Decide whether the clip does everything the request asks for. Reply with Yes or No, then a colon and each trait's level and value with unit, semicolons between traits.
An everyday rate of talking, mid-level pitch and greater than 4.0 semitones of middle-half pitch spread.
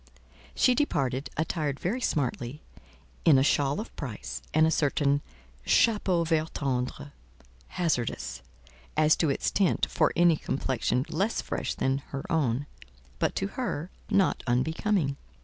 No: slow, 130 wpm; medium, 145 Hz; average, 4.5 semitones